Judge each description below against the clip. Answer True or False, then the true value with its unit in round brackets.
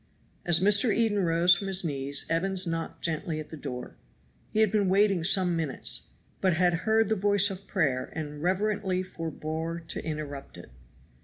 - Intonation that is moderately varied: True (3.7 semitones)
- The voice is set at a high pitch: False (175 Hz)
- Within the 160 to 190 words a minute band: True (170 wpm)